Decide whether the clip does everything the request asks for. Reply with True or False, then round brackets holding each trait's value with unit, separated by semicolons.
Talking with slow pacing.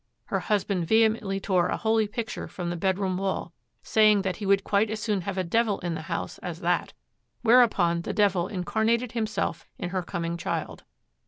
False (185 wpm)